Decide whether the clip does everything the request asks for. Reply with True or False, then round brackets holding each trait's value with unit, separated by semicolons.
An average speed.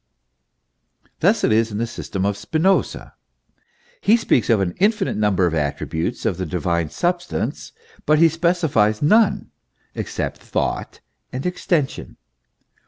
False (130 wpm)